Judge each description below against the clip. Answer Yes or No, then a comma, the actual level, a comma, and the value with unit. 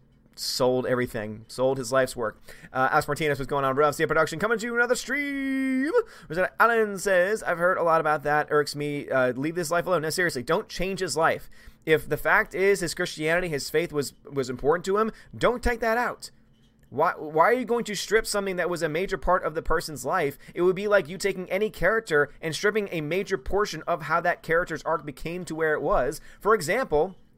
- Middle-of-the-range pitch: Yes, medium, 170 Hz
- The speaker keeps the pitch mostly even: No, average, 5.0 semitones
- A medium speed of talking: No, fast, 225 wpm